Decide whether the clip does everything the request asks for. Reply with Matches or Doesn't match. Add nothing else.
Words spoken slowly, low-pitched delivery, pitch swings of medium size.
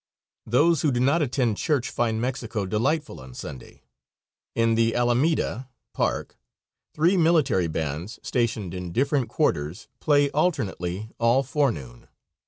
Doesn't match